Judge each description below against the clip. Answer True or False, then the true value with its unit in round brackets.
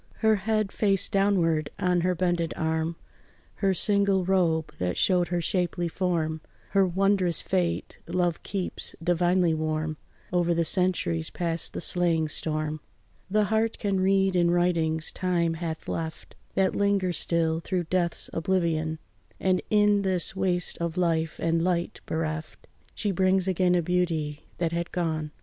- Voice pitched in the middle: True (175 Hz)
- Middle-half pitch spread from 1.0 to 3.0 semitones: True (2.5 semitones)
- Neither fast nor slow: True (145 wpm)